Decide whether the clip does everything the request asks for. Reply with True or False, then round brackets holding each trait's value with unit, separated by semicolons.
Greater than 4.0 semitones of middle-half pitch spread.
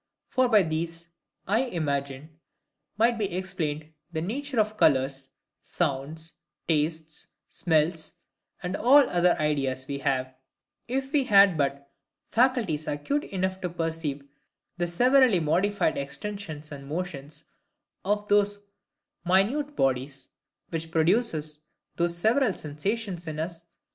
True (5.5 semitones)